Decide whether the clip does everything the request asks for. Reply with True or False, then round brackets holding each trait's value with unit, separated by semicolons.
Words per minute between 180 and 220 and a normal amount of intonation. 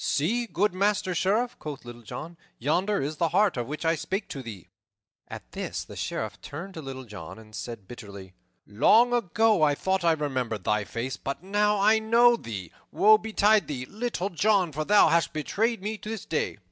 False (190 wpm; 8.3 semitones)